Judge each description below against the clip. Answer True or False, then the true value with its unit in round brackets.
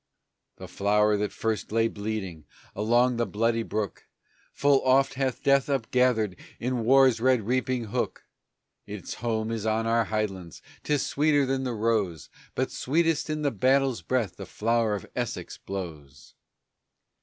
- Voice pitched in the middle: False (115 Hz)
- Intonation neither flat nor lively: True (3.7 semitones)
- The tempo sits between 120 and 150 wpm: True (145 wpm)